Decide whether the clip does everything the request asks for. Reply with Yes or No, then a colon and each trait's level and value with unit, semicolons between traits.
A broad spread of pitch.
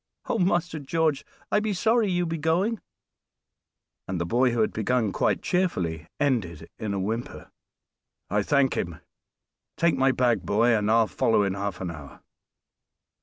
Yes: wide, 8.5 semitones